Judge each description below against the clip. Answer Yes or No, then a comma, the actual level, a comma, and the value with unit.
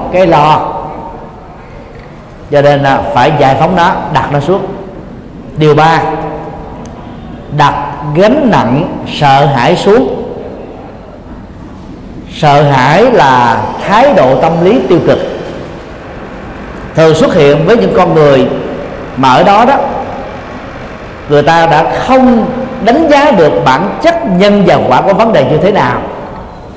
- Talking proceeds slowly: Yes, slow, 130 wpm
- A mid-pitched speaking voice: Yes, medium, 155 Hz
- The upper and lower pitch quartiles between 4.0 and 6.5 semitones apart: Yes, average, 5.1 semitones